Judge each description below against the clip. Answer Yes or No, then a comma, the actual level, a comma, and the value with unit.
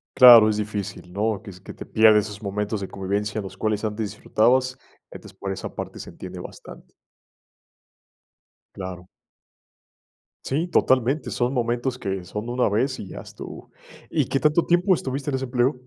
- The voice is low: Yes, low, 110 Hz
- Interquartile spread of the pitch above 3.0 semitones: Yes, average, 4.1 semitones